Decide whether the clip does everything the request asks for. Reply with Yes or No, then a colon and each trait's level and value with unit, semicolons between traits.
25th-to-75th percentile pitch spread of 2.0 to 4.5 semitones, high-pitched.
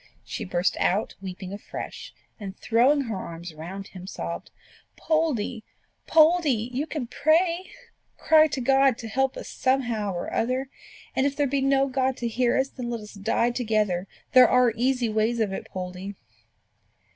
No: average, 5.0 semitones; high, 240 Hz